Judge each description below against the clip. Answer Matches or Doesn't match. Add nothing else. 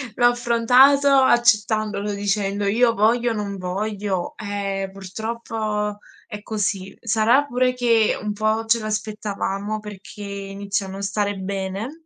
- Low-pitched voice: Doesn't match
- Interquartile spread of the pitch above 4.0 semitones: Doesn't match